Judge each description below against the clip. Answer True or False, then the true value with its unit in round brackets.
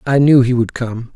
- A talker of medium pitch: False (125 Hz)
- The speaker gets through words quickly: True (260 wpm)